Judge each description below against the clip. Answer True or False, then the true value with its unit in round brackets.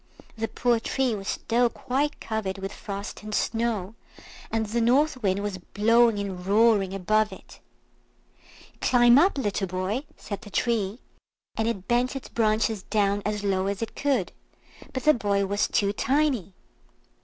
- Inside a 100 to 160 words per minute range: True (155 wpm)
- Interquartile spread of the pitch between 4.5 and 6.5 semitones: False (3.2 semitones)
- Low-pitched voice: False (215 Hz)